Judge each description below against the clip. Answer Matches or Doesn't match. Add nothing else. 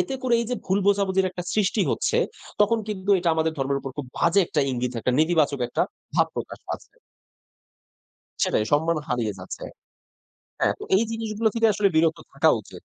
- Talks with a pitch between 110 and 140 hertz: Doesn't match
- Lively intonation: Matches